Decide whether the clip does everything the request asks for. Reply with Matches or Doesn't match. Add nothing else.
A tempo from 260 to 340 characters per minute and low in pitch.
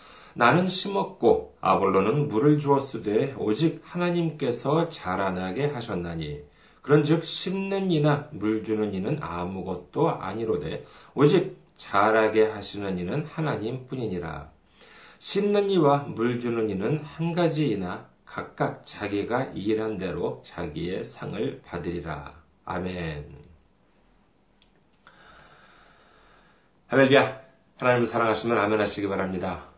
Doesn't match